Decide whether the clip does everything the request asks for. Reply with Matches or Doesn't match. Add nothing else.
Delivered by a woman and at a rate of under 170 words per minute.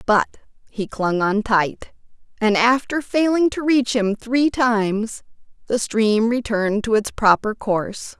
Matches